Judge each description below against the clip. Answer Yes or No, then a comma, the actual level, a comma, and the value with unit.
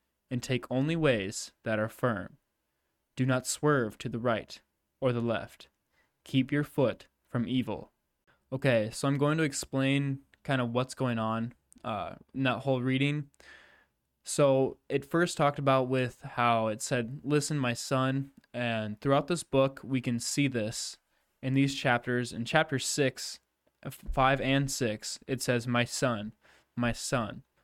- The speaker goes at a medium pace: Yes, average, 155 wpm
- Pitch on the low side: Yes, low, 130 Hz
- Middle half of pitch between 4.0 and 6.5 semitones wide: No, average, 2.7 semitones